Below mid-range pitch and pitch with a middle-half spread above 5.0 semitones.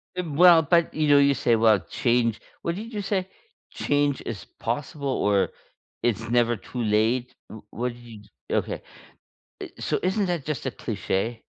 Yes: low, 125 Hz; wide, 5.6 semitones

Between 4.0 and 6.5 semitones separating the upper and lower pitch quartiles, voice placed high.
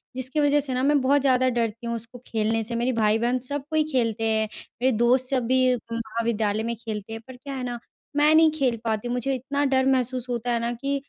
No: narrow, 2.5 semitones; high, 245 Hz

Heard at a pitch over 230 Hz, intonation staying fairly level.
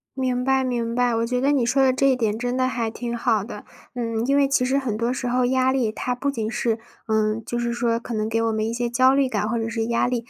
Yes: high, 240 Hz; narrow, 2.1 semitones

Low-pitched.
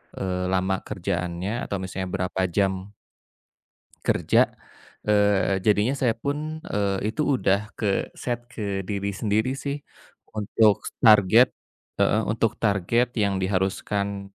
Yes: low, 100 Hz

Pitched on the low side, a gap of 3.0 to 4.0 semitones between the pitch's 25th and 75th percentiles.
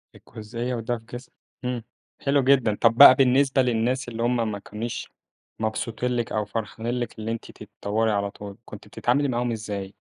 No: low, 115 Hz; narrow, 2.5 semitones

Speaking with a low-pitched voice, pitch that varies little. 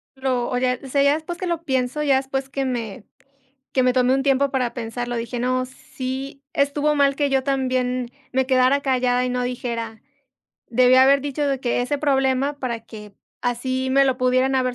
No: very high, 260 Hz; narrow, 1.7 semitones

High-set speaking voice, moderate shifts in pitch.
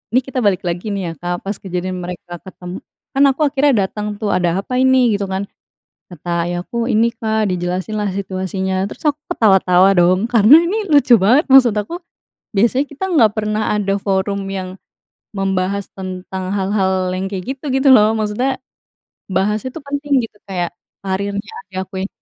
Yes: high, 200 Hz; average, 3.4 semitones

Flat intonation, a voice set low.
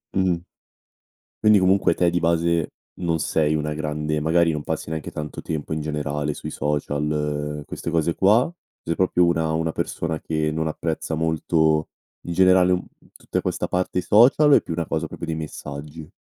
Yes: narrow, 2.3 semitones; very low, 80 Hz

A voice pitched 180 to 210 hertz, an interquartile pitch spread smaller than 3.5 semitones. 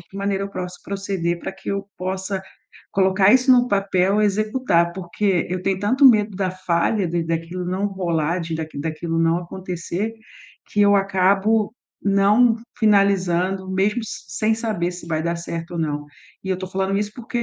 Yes: high, 190 Hz; average, 2.8 semitones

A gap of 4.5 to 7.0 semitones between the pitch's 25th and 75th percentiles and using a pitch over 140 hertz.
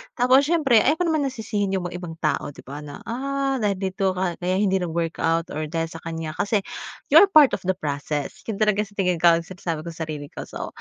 Yes: wide, 5.4 semitones; medium, 185 Hz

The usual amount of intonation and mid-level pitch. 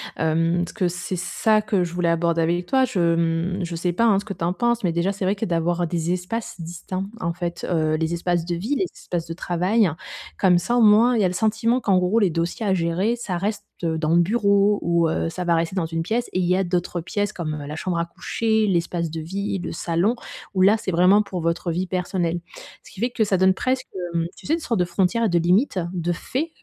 Yes: average, 3.4 semitones; medium, 180 Hz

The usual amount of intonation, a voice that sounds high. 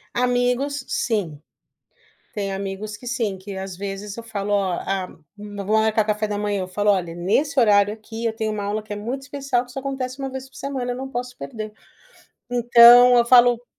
Yes: average, 3.4 semitones; high, 220 Hz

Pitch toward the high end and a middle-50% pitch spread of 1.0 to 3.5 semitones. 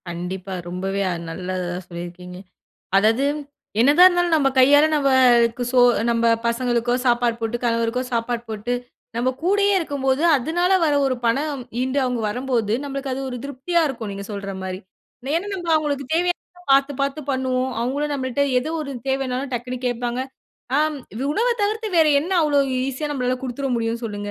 No: very high, 255 Hz; average, 3.9 semitones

